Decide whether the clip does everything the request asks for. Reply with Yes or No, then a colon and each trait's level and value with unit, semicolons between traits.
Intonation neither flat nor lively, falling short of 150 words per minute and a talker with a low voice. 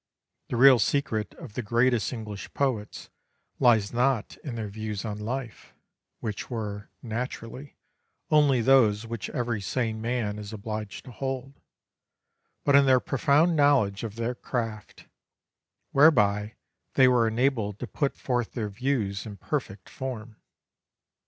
Yes: average, 3.8 semitones; slow, 135 wpm; low, 115 Hz